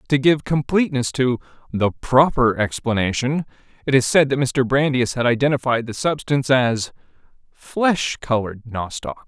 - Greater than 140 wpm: No, slow, 135 wpm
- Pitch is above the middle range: No, low, 130 Hz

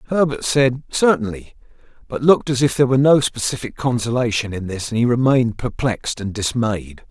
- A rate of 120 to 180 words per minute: Yes, average, 160 wpm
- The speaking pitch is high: No, low, 120 Hz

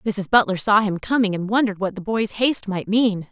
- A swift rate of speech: Yes, fast, 235 wpm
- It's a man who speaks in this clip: No, female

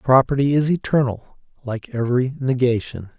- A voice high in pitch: No, low, 130 Hz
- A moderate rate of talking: No, slow, 115 wpm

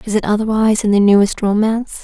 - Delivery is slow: No, fast, 205 wpm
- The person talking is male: No, female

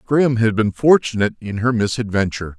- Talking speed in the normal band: Yes, average, 165 wpm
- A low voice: Yes, low, 115 Hz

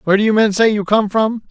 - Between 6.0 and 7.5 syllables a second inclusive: Yes, 6.5 syllables/s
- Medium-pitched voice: No, high, 210 Hz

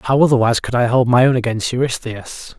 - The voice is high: No, low, 120 Hz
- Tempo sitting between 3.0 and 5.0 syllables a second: No, 5.9 syllables/s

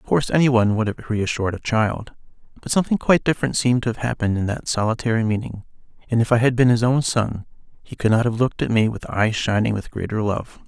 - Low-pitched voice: Yes, low, 115 Hz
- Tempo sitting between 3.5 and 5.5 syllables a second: No, 6.7 syllables/s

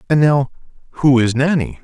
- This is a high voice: No, medium, 140 Hz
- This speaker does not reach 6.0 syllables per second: Yes, 5.3 syllables/s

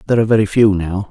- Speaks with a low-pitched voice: Yes, low, 105 Hz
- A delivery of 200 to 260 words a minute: No, fast, 270 wpm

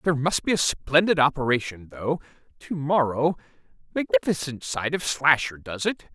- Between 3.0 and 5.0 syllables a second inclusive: Yes, 4.9 syllables/s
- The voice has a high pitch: No, medium, 145 Hz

